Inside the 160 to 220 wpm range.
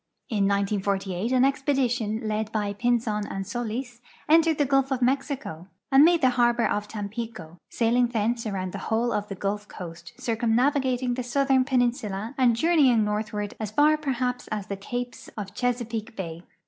Yes: average, 170 wpm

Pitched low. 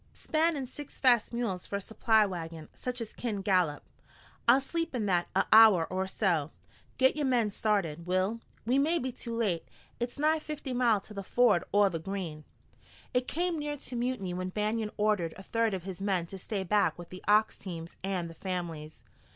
No: high, 210 Hz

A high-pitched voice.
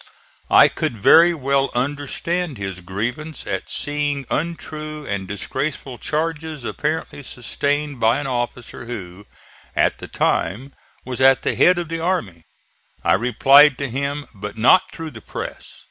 No: medium, 140 Hz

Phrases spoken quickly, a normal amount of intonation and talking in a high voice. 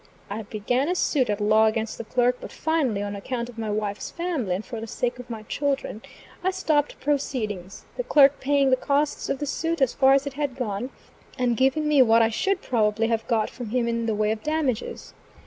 Yes: fast, 220 wpm; average, 4.5 semitones; high, 245 Hz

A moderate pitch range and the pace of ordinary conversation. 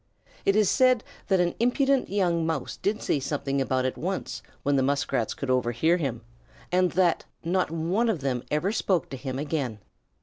No: wide, 5.8 semitones; average, 180 wpm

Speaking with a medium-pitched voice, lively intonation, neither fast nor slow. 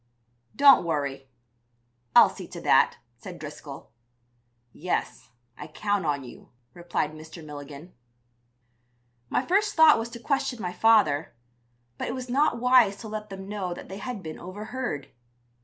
No: high, 195 Hz; wide, 7.6 semitones; average, 145 wpm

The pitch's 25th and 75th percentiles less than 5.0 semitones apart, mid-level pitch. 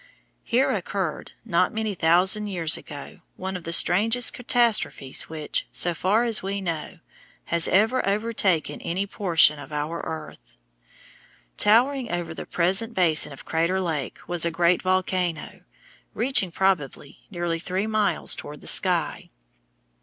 Yes: average, 4.3 semitones; medium, 180 Hz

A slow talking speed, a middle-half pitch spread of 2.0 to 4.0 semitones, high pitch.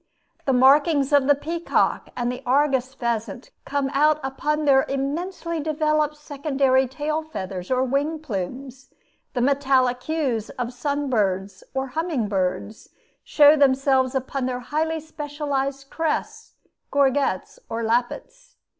Yes: slow, 130 wpm; average, 3.2 semitones; very high, 275 Hz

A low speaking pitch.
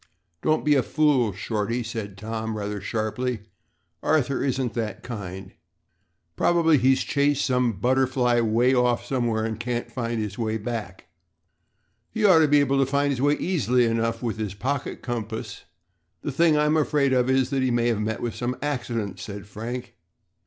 Yes: low, 120 Hz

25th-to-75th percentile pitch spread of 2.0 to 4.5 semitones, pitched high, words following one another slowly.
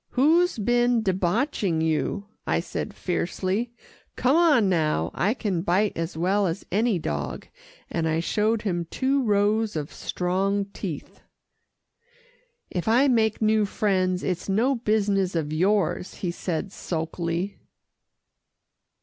Yes: average, 4.1 semitones; high, 195 Hz; slow, 125 wpm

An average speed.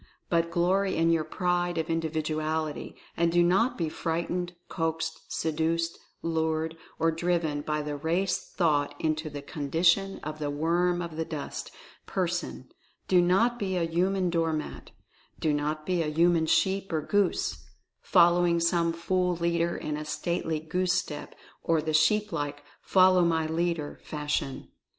Yes: average, 155 wpm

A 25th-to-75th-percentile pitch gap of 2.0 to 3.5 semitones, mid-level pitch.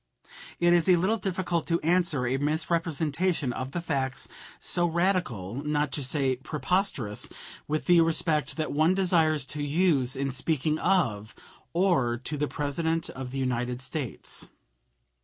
No: average, 4.5 semitones; medium, 150 Hz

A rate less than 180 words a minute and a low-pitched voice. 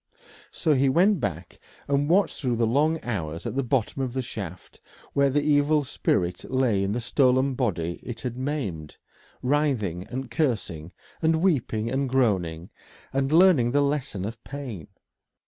Yes: average, 160 wpm; low, 130 Hz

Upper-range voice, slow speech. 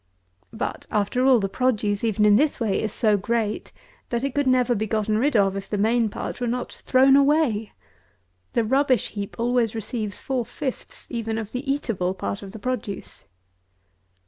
No: high, 230 Hz; average, 180 wpm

